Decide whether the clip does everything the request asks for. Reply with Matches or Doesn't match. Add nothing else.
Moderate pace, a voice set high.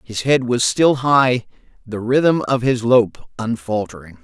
Doesn't match